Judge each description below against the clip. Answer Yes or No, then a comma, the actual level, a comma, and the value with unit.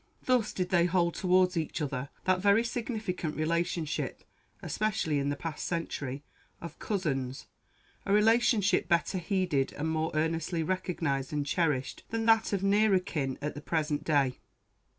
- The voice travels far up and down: No, average, 4.8 semitones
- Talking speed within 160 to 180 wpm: No, average, 150 wpm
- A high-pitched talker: No, medium, 170 Hz